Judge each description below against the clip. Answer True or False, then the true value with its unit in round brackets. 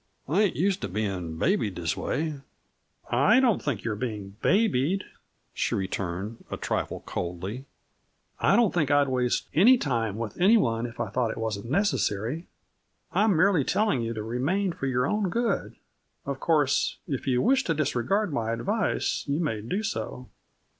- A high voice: False (135 Hz)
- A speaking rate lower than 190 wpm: True (175 wpm)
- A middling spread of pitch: False (9.0 semitones)